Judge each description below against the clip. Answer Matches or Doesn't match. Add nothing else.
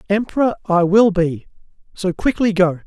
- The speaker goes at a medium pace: Matches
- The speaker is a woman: Doesn't match